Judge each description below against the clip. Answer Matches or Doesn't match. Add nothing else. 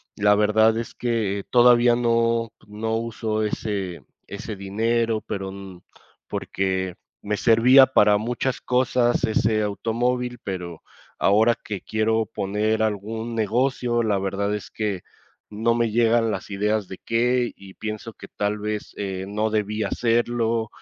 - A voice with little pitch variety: Matches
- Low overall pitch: Matches